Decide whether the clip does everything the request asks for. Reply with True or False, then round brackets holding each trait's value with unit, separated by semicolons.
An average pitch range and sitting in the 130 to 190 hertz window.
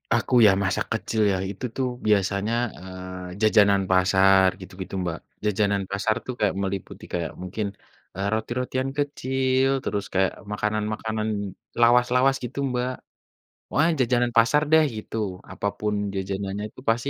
False (4.1 semitones; 105 Hz)